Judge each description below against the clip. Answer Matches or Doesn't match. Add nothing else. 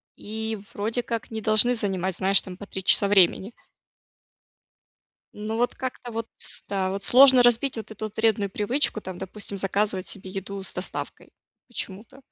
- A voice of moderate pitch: Doesn't match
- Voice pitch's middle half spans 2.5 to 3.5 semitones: Matches